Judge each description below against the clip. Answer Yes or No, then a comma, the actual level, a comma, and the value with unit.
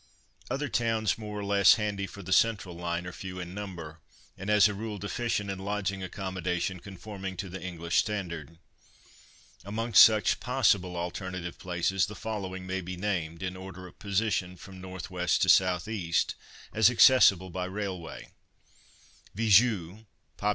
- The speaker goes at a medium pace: Yes, average, 150 wpm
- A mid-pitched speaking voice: No, very low, 95 Hz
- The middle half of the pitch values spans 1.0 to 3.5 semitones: Yes, narrow, 2.6 semitones